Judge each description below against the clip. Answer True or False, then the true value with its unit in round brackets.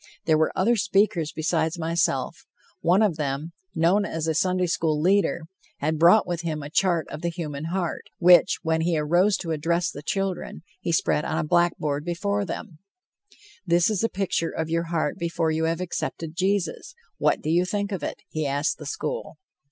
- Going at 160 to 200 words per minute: True (190 wpm)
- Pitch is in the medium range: True (170 Hz)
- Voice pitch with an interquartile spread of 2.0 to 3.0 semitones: True (2.6 semitones)